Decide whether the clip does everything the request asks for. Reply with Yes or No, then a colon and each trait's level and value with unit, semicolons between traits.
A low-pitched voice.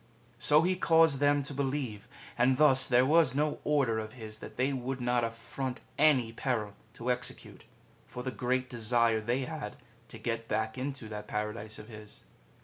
Yes: low, 125 Hz